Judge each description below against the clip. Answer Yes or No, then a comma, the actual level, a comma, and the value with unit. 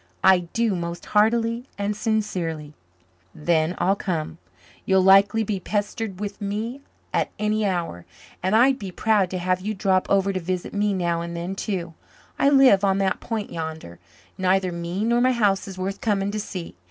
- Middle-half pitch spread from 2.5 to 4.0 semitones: Yes, average, 3.1 semitones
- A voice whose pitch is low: No, high, 195 Hz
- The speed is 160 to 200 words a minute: Yes, average, 175 wpm